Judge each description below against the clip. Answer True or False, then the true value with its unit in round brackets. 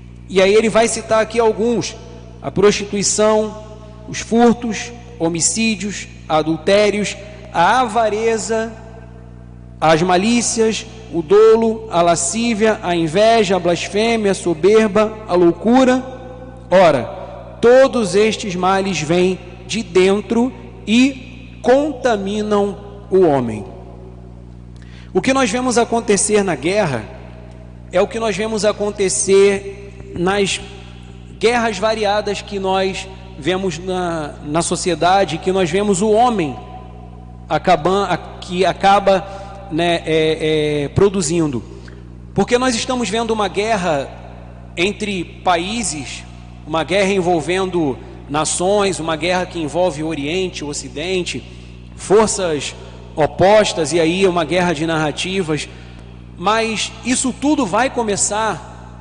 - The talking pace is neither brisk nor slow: False (110 wpm)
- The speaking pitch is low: False (185 Hz)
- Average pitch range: False (6.6 semitones)